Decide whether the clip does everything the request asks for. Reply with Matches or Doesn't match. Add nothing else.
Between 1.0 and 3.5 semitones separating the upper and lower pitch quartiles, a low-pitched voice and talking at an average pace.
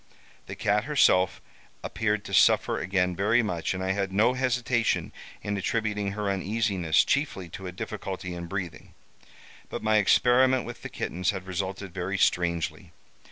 Matches